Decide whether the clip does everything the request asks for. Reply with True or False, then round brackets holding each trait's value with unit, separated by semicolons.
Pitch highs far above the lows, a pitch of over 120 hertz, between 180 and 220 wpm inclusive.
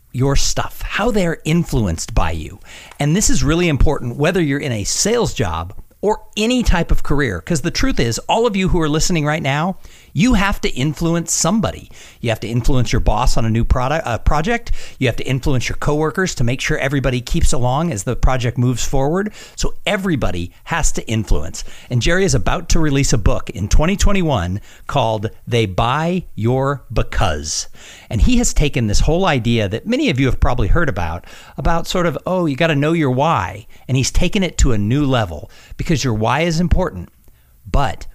True (7.0 semitones; 135 Hz; 200 wpm)